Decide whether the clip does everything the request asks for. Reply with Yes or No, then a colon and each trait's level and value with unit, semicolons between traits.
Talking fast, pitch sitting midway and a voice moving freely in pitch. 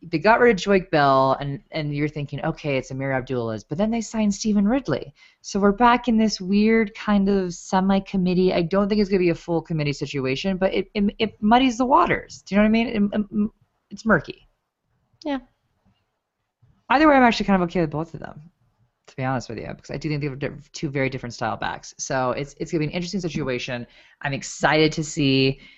Yes: fast, 220 wpm; medium, 175 Hz; wide, 6.6 semitones